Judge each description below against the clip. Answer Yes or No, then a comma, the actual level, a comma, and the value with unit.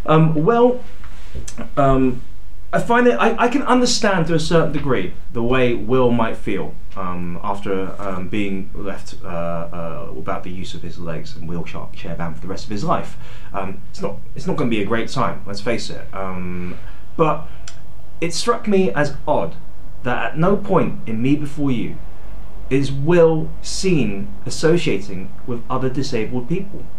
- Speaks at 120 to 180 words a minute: Yes, average, 175 wpm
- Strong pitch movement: Yes, wide, 8.4 semitones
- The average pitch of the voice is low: Yes, low, 125 Hz